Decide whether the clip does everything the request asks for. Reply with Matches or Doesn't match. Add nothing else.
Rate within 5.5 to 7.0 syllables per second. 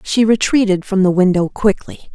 Doesn't match